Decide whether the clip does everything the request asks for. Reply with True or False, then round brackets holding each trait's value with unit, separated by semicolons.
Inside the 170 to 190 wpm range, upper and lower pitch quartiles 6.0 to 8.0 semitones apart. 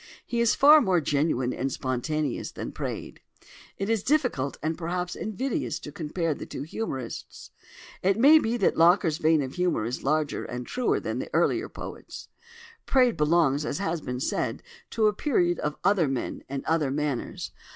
True (175 wpm; 6.5 semitones)